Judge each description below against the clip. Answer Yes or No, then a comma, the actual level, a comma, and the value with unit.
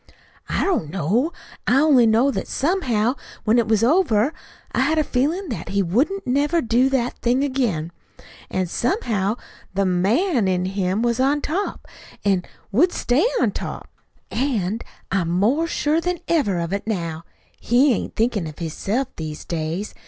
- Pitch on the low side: No, high, 235 Hz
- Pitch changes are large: Yes, wide, 6.8 semitones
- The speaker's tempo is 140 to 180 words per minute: Yes, average, 160 wpm